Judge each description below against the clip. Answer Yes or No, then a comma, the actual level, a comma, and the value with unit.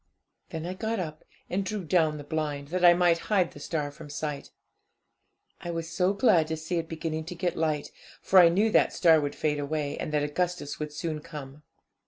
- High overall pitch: No, medium, 160 Hz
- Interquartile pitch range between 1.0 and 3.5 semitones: Yes, average, 2.9 semitones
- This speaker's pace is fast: Yes, fast, 215 wpm